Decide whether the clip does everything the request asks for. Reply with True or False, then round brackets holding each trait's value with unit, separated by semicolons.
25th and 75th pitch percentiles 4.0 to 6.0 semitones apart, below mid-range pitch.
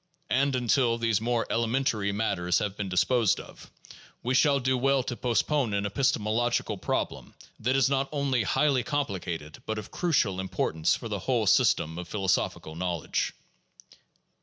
True (5.0 semitones; 115 Hz)